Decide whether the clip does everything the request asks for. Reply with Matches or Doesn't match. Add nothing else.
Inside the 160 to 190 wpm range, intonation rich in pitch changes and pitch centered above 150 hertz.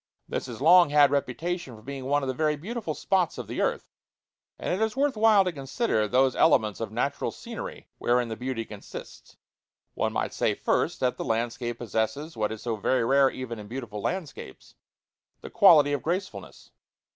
Doesn't match